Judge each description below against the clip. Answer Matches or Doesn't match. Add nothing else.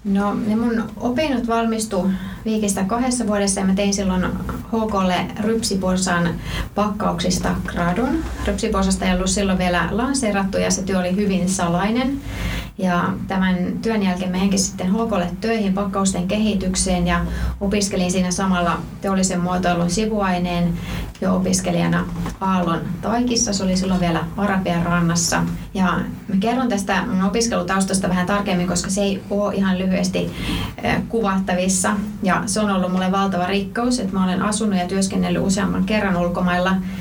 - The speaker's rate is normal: Matches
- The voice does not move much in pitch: Matches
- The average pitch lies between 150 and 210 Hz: Matches